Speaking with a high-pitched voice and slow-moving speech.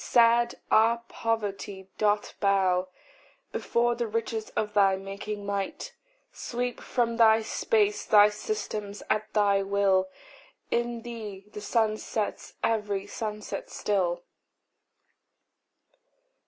Yes: high, 210 Hz; slow, 105 wpm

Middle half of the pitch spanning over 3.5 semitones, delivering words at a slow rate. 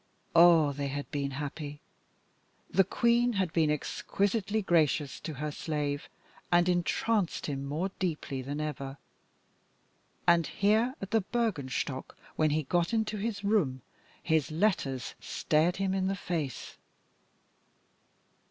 Yes: average, 5.3 semitones; slow, 125 wpm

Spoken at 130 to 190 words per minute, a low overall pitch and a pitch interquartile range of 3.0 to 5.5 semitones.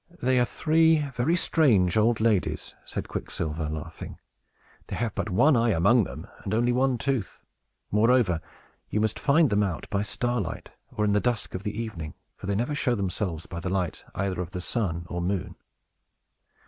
Yes: average, 180 wpm; low, 105 Hz; average, 5.1 semitones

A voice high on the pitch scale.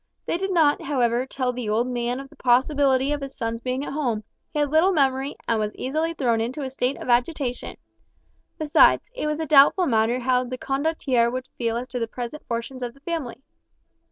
Yes: very high, 260 Hz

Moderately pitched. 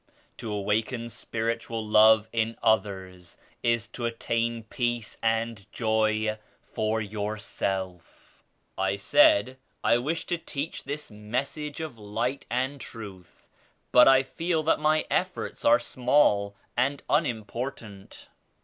No: low, 115 Hz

